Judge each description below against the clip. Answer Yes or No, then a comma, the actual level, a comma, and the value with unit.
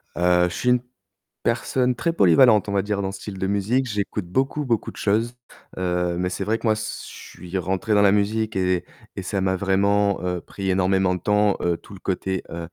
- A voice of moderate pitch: No, low, 100 Hz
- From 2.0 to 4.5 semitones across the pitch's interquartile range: Yes, average, 2.7 semitones